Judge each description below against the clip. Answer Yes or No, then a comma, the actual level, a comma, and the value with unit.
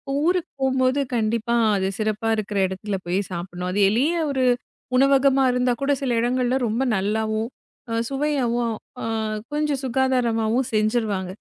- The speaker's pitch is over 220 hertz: Yes, high, 235 Hz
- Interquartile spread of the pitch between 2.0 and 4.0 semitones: Yes, average, 3.6 semitones